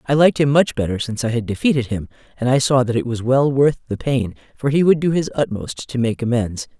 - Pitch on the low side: Yes, low, 125 Hz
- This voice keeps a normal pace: No, fast, 255 wpm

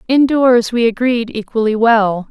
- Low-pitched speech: No, high, 230 Hz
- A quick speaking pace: No, slow, 130 wpm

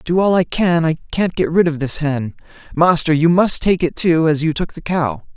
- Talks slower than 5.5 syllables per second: Yes, 5.0 syllables/s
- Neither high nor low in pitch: Yes, medium, 165 Hz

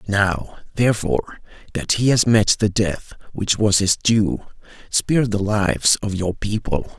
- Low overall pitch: Yes, low, 105 Hz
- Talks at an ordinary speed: Yes, average, 155 wpm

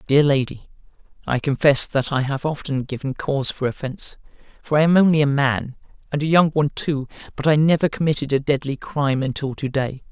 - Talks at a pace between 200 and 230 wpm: No, average, 190 wpm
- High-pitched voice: No, medium, 140 Hz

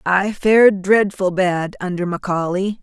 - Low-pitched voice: No, high, 190 Hz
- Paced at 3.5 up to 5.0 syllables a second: Yes, 4.5 syllables/s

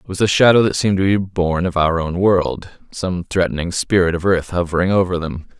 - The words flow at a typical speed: No, fast, 215 wpm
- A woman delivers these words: No, male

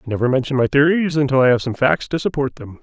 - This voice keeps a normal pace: No, fast, 275 wpm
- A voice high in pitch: No, low, 135 Hz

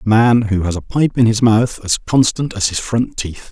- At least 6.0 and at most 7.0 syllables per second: No, 4.8 syllables/s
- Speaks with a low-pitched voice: Yes, low, 110 Hz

